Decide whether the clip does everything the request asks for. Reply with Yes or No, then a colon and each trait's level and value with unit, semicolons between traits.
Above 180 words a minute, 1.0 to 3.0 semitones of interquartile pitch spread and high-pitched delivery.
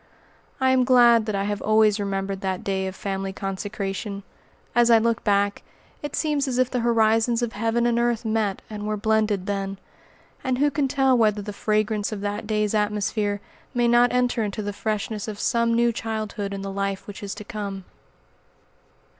Yes: average, 190 wpm; average, 2.7 semitones; high, 215 Hz